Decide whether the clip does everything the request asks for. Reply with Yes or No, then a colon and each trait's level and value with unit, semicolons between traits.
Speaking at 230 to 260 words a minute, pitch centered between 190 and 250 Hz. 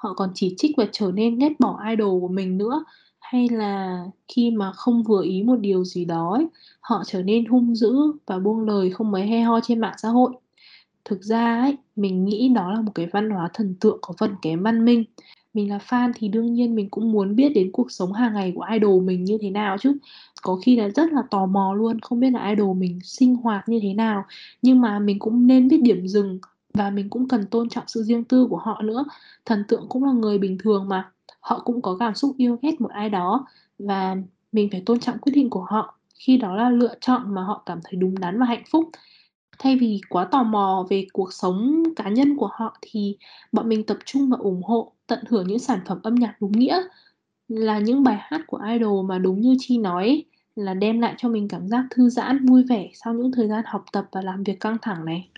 Yes: average, 240 wpm; high, 220 Hz